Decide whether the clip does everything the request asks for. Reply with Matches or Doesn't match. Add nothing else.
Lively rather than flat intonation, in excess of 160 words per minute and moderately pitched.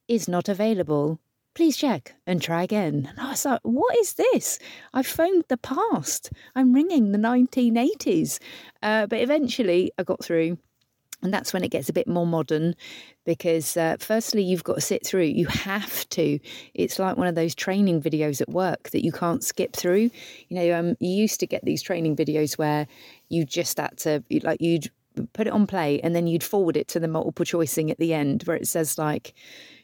Matches